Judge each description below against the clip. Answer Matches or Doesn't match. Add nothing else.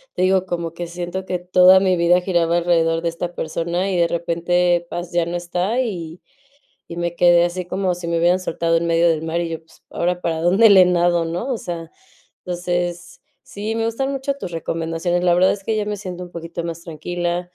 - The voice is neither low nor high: Matches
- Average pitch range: Doesn't match